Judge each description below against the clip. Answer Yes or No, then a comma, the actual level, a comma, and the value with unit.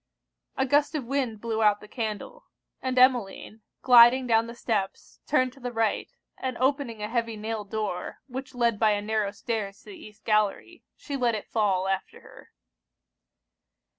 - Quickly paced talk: No, average, 170 wpm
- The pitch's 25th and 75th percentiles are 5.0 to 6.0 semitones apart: No, average, 3.4 semitones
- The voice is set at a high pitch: Yes, high, 230 Hz